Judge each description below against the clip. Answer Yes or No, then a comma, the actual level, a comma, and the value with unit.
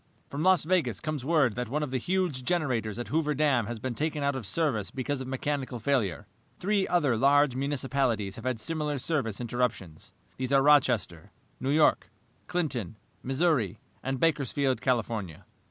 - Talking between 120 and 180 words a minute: Yes, average, 165 wpm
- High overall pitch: No, low, 135 Hz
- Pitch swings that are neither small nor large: Yes, average, 4.1 semitones